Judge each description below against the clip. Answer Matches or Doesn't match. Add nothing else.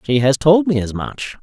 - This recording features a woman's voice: Doesn't match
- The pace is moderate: Doesn't match